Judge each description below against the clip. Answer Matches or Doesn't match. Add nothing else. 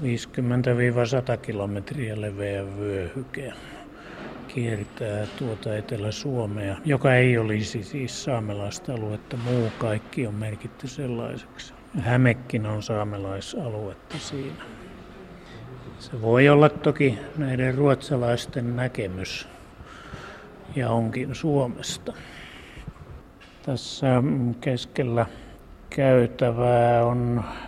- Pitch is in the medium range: Doesn't match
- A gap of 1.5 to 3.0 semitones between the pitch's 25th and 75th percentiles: Doesn't match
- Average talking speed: Doesn't match